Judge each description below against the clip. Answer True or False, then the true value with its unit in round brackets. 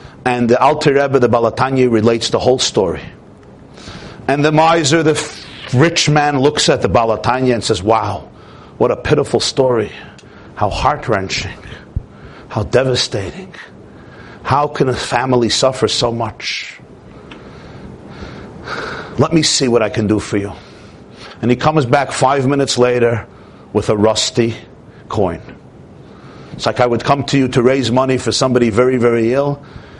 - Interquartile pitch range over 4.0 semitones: False (3.3 semitones)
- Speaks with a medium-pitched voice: False (125 Hz)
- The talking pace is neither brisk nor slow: True (150 wpm)